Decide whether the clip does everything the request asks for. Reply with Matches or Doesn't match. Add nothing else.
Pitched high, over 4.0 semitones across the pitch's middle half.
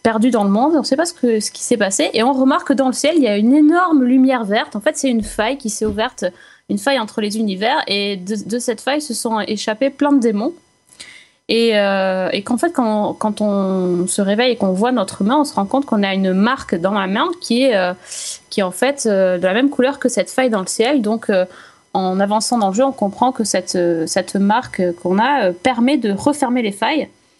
Matches